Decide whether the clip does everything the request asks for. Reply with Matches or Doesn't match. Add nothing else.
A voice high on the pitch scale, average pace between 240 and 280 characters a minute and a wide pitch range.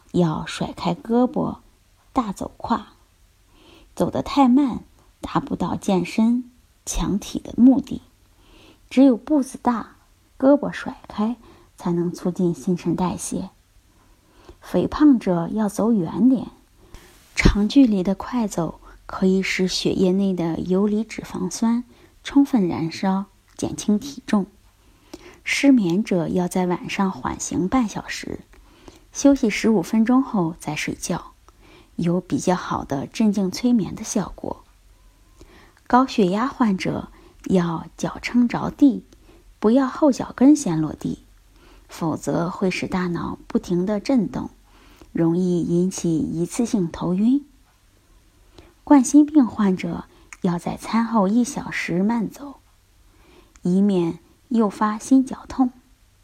Doesn't match